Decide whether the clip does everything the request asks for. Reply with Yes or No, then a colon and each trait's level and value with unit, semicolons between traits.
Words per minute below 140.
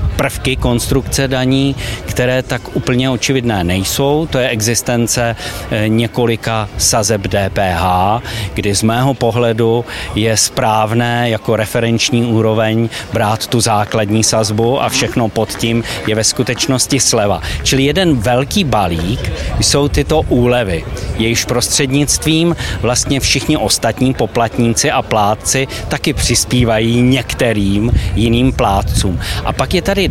Yes: average, 120 wpm